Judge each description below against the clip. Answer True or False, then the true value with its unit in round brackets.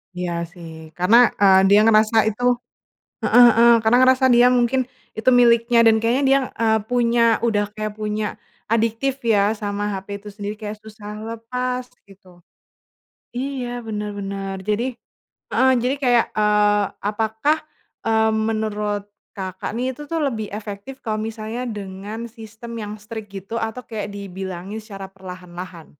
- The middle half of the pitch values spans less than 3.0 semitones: True (2.6 semitones)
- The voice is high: True (220 Hz)